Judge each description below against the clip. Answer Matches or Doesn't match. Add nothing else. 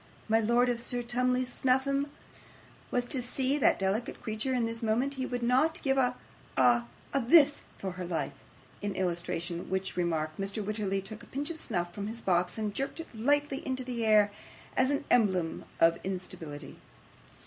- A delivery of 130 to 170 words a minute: Doesn't match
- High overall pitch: Matches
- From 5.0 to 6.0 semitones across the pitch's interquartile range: Matches